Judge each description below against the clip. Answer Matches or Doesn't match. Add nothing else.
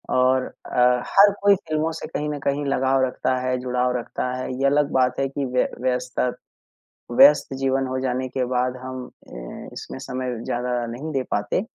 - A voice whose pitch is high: Doesn't match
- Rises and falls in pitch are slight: Matches